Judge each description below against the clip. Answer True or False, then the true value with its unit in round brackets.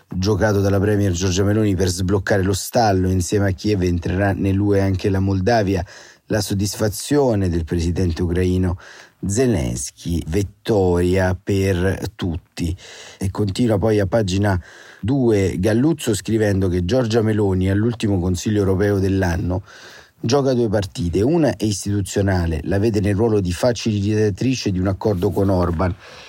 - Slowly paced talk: False (130 wpm)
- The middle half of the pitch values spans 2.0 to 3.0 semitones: True (2.6 semitones)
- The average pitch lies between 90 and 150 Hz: True (100 Hz)